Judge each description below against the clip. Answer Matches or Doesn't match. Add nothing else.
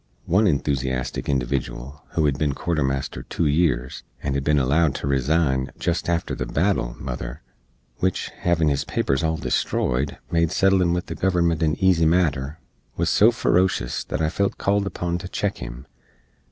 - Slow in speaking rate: Doesn't match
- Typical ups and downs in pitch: Matches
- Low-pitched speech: Matches